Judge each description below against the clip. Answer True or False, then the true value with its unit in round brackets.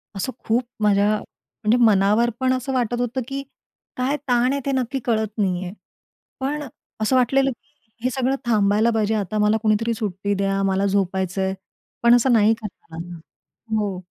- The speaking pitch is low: False (220 Hz)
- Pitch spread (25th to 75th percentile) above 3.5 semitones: True (4.1 semitones)